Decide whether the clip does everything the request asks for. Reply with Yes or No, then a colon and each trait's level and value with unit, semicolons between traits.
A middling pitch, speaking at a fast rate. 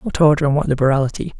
Yes: medium, 145 Hz; fast, 215 wpm